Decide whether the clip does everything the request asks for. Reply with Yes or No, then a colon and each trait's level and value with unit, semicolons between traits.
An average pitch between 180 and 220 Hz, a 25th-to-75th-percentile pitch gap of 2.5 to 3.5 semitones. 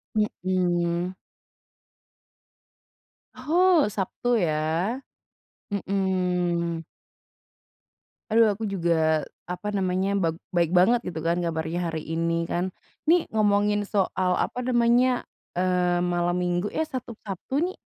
No: medium, 185 Hz; average, 4.2 semitones